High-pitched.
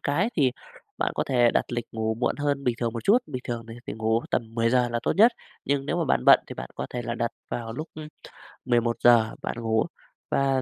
No: low, 120 Hz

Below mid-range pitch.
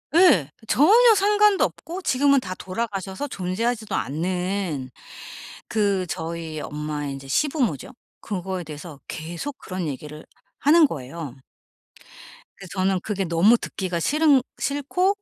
No: high, 190 Hz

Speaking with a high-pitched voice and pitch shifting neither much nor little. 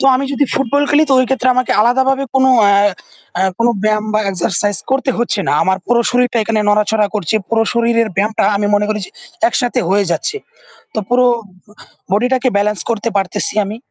Yes: high, 230 Hz; average, 3.6 semitones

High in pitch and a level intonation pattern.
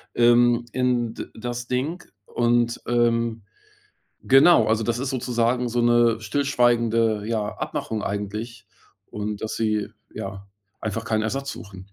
No: low, 115 Hz; narrow, 1.7 semitones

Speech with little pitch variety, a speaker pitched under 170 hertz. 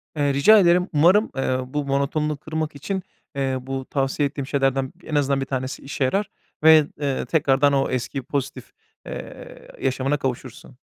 Yes: narrow, 2.3 semitones; medium, 140 Hz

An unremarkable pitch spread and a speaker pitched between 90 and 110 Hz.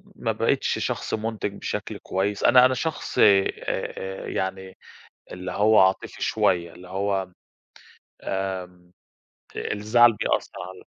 No: narrow, 2.2 semitones; very low, 95 Hz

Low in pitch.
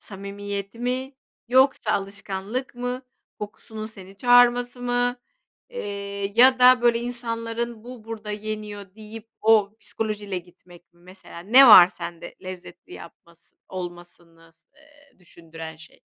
No: high, 210 Hz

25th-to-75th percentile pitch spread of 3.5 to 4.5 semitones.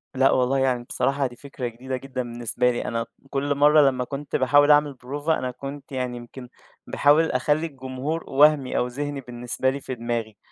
No: narrow, 2.6 semitones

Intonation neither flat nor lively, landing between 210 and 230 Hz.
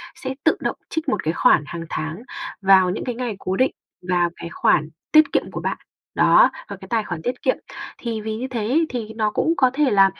No: wide, 5.7 semitones; high, 220 Hz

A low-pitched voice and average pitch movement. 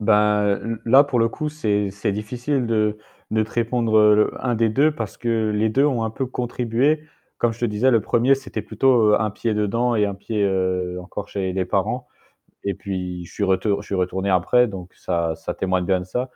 Yes: low, 110 Hz; average, 3.3 semitones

